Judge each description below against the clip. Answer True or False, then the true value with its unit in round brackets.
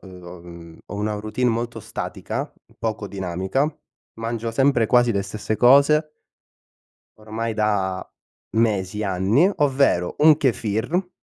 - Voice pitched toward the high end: False (110 Hz)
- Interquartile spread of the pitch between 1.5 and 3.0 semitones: False (4.2 semitones)